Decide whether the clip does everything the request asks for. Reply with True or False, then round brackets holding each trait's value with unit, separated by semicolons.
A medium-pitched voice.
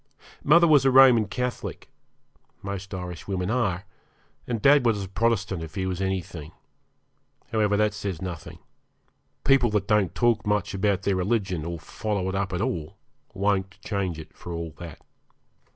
False (100 Hz)